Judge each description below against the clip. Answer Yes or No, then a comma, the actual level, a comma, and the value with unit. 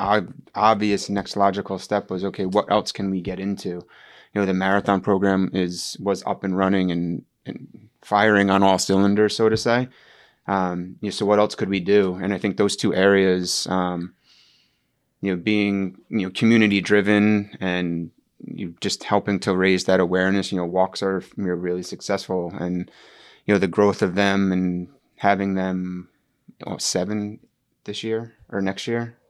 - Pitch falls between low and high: No, very low, 95 Hz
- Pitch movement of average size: No, narrow, 1.8 semitones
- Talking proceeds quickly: No, average, 175 wpm